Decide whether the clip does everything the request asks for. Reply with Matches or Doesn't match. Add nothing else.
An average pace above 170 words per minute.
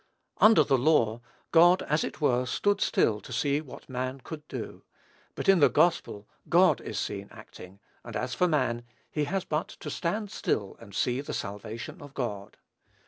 Matches